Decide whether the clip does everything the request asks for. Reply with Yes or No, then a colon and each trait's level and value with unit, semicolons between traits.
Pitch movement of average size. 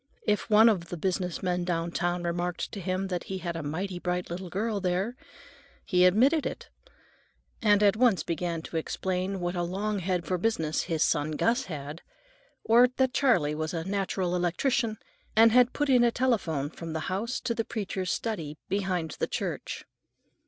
Yes: average, 4.1 semitones